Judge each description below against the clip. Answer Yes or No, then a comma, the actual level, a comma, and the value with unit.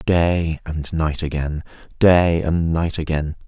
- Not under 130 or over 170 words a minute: Yes, average, 140 wpm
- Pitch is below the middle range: Yes, very low, 80 Hz